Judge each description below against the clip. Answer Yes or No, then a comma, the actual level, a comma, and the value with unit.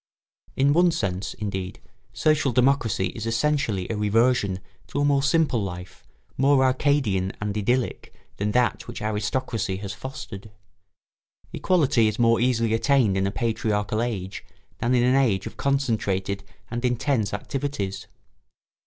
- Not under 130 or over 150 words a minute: Yes, slow, 135 wpm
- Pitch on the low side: Yes, low, 115 Hz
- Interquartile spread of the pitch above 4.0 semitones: Yes, average, 4.9 semitones